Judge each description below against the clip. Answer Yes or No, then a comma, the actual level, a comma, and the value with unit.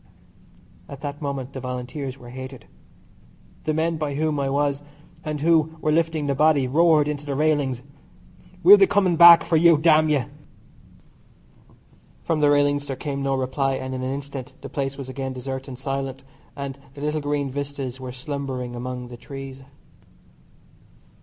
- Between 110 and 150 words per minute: No, average, 165 wpm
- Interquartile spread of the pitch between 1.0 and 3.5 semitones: Yes, narrow, 2.4 semitones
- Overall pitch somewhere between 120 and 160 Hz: Yes, medium, 140 Hz